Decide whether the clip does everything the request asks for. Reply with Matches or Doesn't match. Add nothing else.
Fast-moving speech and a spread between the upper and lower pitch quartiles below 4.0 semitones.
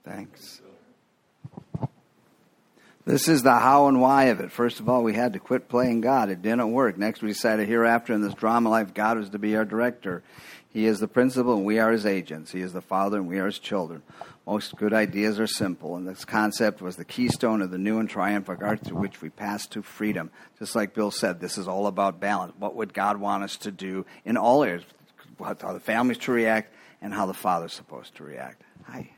Matches